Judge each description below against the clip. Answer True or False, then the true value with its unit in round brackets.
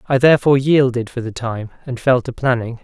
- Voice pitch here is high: False (125 Hz)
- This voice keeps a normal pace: False (210 wpm)